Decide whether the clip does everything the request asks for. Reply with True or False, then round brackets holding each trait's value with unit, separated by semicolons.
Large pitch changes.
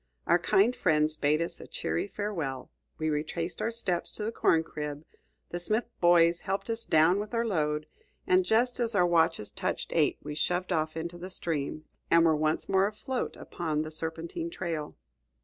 False (4.3 semitones)